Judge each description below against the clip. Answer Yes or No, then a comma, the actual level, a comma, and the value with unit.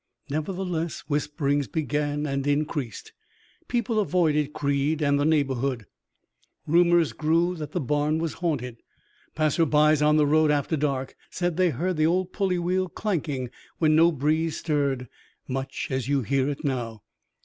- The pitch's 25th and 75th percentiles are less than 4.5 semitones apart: Yes, average, 3.0 semitones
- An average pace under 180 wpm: Yes, average, 150 wpm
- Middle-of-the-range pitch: Yes, medium, 150 Hz